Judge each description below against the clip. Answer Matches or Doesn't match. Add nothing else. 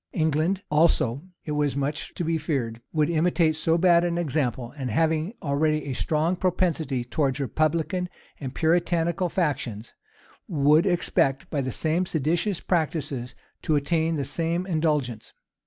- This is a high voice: Doesn't match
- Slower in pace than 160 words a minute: Matches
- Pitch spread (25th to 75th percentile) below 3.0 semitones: Doesn't match